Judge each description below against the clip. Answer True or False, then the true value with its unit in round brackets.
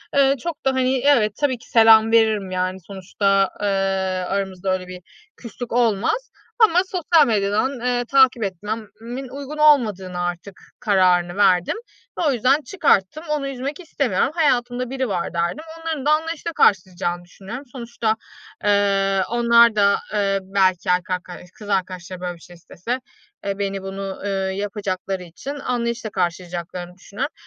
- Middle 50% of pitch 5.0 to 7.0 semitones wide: True (5.5 semitones)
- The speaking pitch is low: False (210 Hz)